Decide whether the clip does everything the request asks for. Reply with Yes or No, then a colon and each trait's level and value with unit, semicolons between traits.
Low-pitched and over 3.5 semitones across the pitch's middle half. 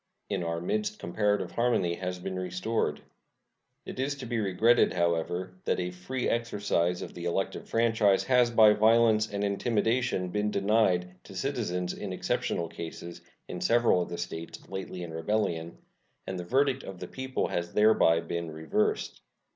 Yes: very low, 95 Hz; average, 4.6 semitones